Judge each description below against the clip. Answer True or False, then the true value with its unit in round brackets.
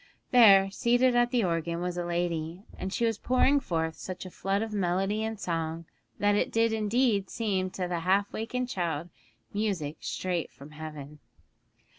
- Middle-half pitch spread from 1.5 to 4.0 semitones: False (4.7 semitones)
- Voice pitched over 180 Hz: True (190 Hz)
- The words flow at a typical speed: True (170 wpm)